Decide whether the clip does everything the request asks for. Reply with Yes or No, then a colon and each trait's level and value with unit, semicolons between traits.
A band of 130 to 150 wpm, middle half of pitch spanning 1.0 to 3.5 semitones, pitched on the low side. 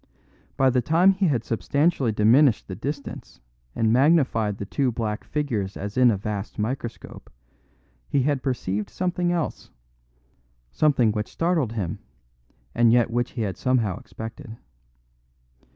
No: slow, 135 wpm; average, 4.9 semitones; low, 120 Hz